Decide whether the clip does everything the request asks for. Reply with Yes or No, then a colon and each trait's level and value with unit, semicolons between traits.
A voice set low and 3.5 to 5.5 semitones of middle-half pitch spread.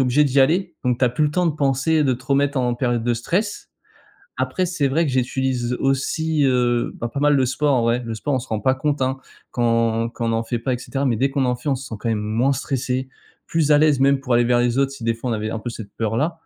No: low, 130 Hz; average, 3.0 semitones